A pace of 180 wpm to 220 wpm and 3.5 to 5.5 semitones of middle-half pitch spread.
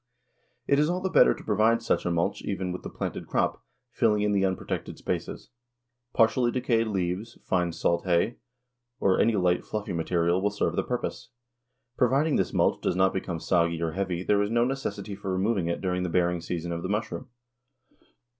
Yes: average, 190 wpm; average, 4.4 semitones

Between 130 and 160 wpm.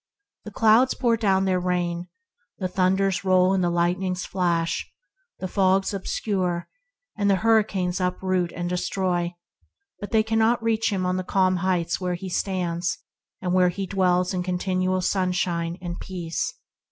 Yes: average, 150 wpm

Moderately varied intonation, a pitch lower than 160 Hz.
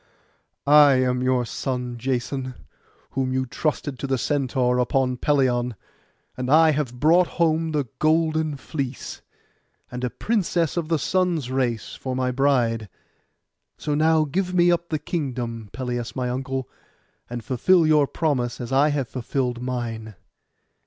Yes: average, 3.8 semitones; low, 135 Hz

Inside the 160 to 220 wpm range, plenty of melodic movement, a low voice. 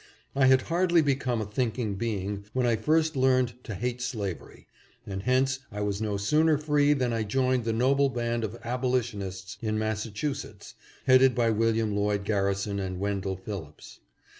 No: average, 165 wpm; average, 4.2 semitones; low, 115 Hz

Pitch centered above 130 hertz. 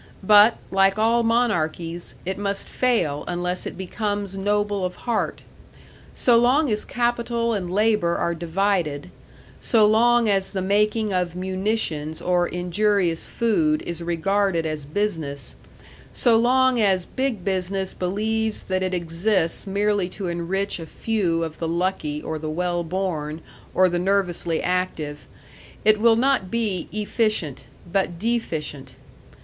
Yes: high, 190 Hz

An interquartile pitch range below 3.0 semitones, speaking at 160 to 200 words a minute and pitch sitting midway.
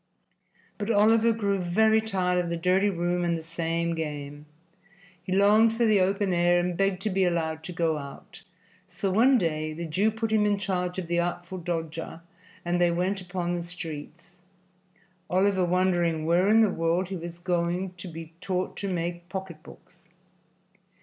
Yes: narrow, 2.5 semitones; average, 175 wpm; medium, 180 Hz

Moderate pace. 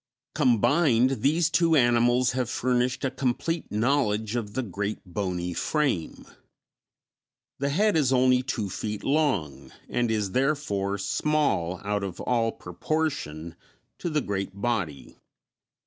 No: slow, 125 wpm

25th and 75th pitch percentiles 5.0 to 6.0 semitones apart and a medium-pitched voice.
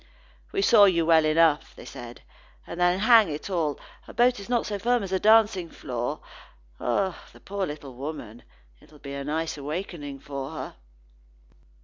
Yes: wide, 5.6 semitones; medium, 165 Hz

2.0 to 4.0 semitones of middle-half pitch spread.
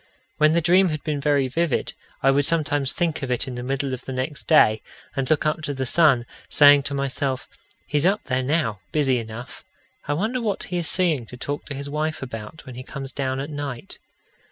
Yes: average, 3.1 semitones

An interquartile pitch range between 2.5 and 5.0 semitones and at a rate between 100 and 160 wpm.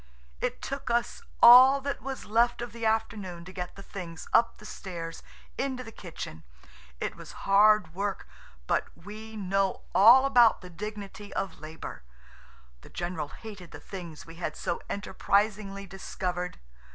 Yes: average, 3.9 semitones; average, 150 wpm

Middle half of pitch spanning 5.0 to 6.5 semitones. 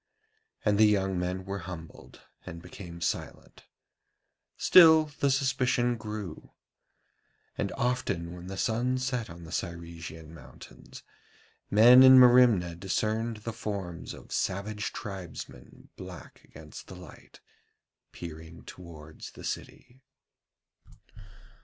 Yes: wide, 5.6 semitones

